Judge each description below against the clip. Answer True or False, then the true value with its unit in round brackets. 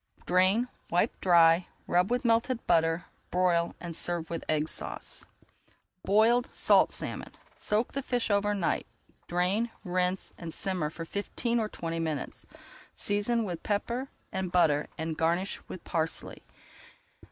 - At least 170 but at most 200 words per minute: False (135 wpm)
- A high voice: False (180 Hz)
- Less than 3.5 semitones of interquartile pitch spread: False (4.3 semitones)